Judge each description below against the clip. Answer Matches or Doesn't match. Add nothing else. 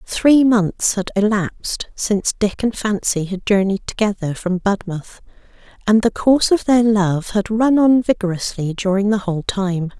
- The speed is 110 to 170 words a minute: Matches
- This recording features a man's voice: Doesn't match